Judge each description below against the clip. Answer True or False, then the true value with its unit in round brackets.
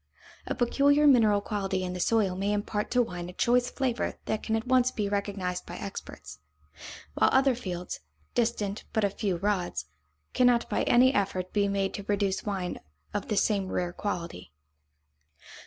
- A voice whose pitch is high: True (205 Hz)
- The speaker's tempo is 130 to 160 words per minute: False (170 wpm)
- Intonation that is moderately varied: True (3.9 semitones)